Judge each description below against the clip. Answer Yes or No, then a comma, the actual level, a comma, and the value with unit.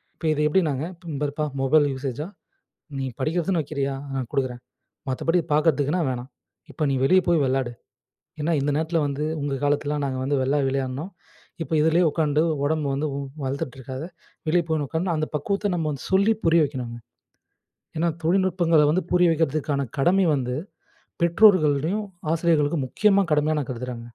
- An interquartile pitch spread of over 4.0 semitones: No, average, 3.5 semitones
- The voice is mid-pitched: Yes, medium, 150 Hz